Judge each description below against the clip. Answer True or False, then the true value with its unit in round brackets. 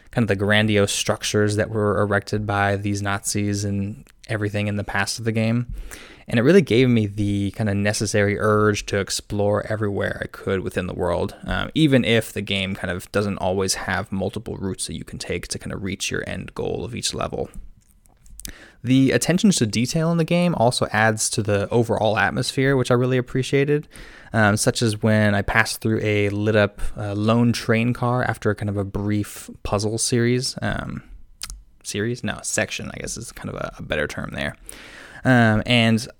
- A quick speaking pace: False (195 wpm)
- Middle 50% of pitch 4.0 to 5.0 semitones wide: False (2.7 semitones)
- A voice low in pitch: True (105 Hz)